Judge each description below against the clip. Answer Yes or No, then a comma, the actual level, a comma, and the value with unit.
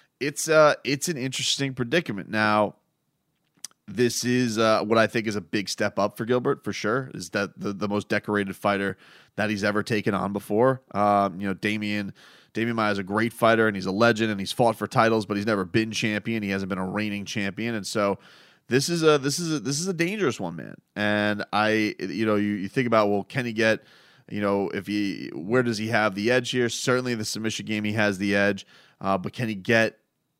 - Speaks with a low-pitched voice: Yes, low, 110 Hz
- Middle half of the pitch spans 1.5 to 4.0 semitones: Yes, average, 2.7 semitones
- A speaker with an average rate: No, fast, 225 wpm